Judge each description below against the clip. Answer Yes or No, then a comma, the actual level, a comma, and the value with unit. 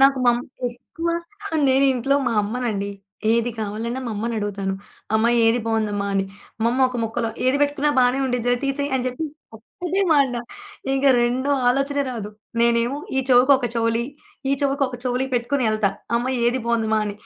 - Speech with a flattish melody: No, average, 3.1 semitones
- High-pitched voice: Yes, high, 245 Hz